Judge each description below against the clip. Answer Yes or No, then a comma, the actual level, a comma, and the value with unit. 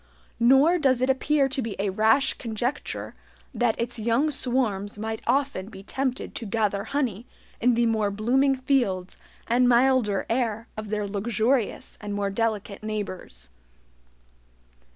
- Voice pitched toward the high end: Yes, high, 230 Hz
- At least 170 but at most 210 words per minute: No, average, 140 wpm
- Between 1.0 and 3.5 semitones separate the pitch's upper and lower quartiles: No, average, 3.9 semitones